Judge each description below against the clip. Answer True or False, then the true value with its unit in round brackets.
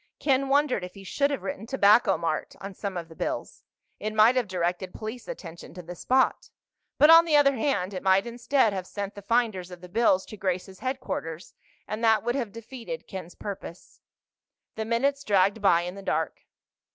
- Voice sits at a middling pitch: False (210 Hz)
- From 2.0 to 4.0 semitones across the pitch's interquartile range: False (5.2 semitones)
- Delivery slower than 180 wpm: False (195 wpm)